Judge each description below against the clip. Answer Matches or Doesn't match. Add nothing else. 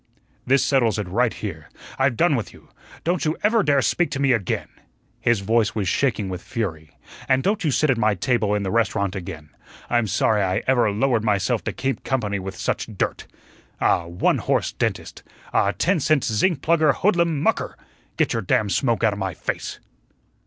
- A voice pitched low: Matches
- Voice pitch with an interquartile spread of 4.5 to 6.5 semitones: Matches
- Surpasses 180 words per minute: Matches